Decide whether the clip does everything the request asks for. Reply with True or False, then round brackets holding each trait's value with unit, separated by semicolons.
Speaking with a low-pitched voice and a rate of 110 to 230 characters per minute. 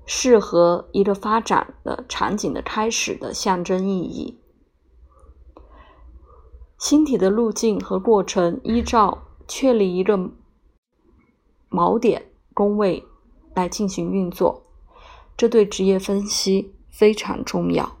False (195 Hz; 165 characters per minute)